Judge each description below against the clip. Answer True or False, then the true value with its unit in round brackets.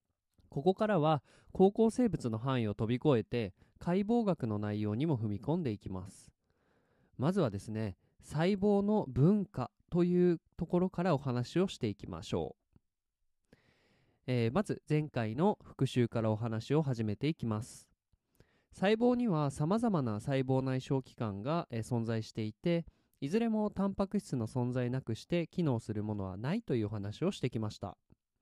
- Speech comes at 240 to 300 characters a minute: False (310 characters per minute)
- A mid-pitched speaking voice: False (130 Hz)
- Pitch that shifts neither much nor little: False (8.0 semitones)